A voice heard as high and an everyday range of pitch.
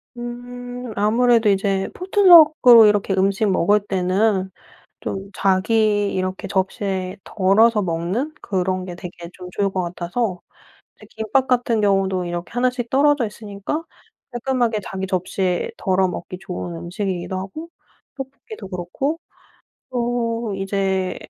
Yes: high, 200 Hz; average, 4.3 semitones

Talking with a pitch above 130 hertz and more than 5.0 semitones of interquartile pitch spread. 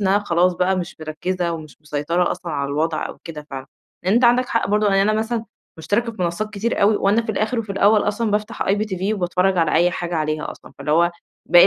No: medium, 185 Hz; average, 3.9 semitones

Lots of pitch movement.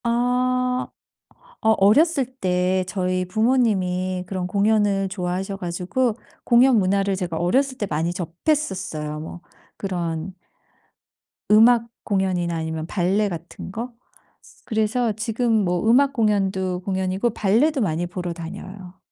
No: average, 4.4 semitones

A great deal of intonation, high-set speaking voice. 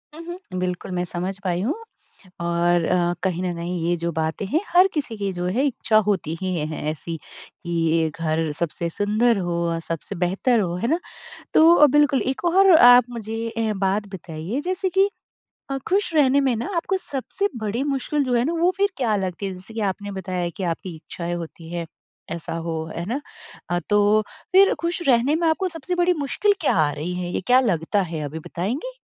Yes: wide, 8.2 semitones; high, 205 Hz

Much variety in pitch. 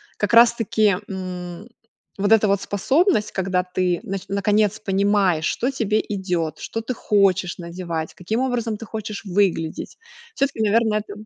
No: average, 3.2 semitones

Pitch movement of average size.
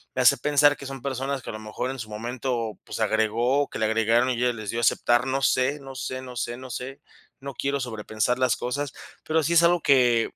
Yes: average, 3.0 semitones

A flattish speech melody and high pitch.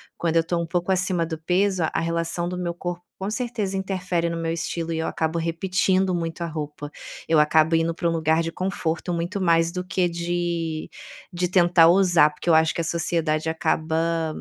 No: narrow, 1.7 semitones; medium, 170 Hz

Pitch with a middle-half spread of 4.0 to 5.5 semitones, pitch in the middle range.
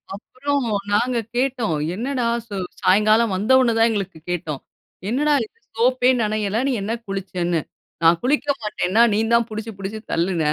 No: average, 4.3 semitones; high, 215 Hz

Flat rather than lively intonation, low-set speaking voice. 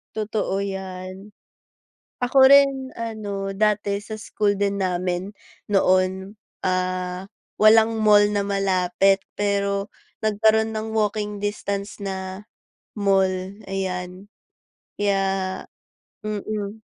No: narrow, 2.0 semitones; high, 200 Hz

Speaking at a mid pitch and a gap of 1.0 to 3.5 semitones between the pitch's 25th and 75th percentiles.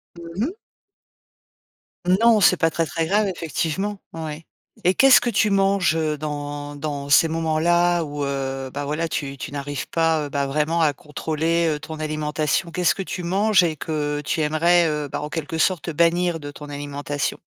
Yes: medium, 160 Hz; average, 2.8 semitones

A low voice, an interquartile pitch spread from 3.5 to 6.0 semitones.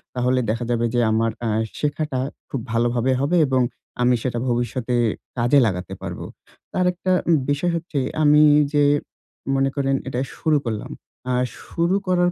Yes: low, 130 Hz; average, 3.8 semitones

